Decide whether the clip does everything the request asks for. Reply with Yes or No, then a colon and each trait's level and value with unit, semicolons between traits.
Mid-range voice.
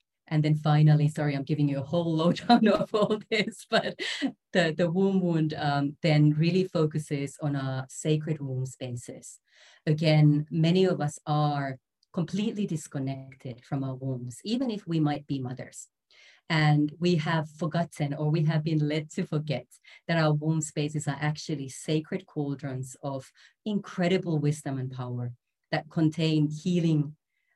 Yes: medium, 155 Hz